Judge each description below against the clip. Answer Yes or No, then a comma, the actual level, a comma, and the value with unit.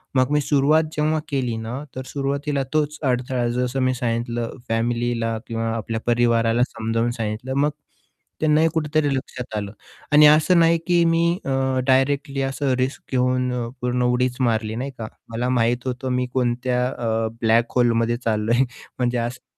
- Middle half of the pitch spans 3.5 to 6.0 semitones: No, average, 2.8 semitones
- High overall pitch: No, low, 125 Hz